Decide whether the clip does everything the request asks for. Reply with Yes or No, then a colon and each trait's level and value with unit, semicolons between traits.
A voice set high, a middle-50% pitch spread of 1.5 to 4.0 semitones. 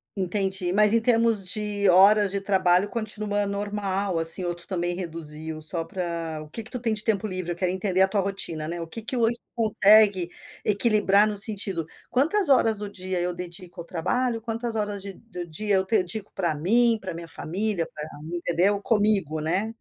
Yes: high, 195 Hz; average, 3.5 semitones